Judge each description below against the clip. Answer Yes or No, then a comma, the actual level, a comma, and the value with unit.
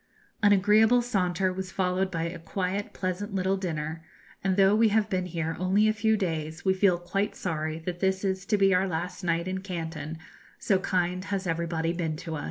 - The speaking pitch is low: No, medium, 185 Hz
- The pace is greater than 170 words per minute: Yes, average, 200 wpm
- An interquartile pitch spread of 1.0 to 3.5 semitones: Yes, average, 2.7 semitones